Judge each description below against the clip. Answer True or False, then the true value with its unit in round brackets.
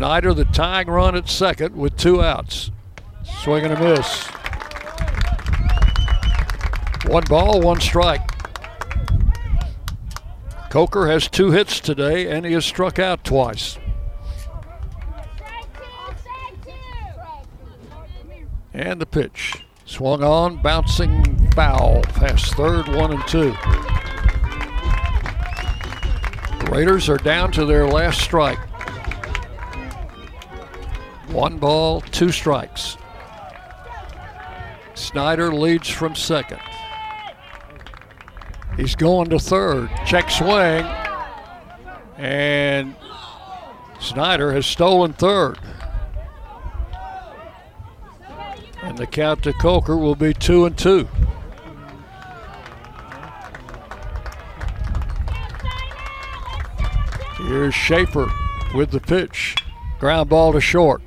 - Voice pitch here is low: True (130 Hz)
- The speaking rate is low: True (85 wpm)